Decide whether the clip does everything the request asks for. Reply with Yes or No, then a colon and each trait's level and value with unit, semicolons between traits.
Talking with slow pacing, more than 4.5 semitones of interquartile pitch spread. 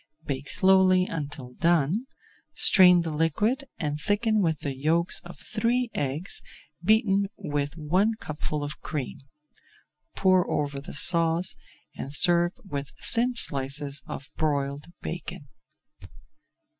Yes: slow, 120 wpm; average, 4.9 semitones